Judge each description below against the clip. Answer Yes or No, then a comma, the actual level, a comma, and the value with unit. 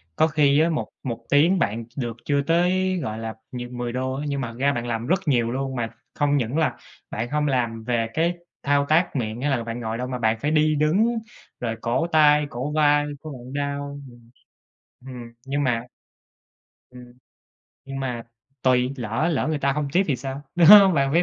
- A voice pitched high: No, low, 135 Hz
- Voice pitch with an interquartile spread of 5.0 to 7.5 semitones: No, average, 3.9 semitones